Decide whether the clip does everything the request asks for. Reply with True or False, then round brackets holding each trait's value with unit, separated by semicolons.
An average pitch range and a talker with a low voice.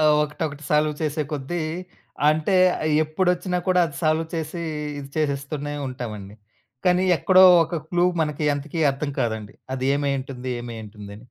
False (3.5 semitones; 150 Hz)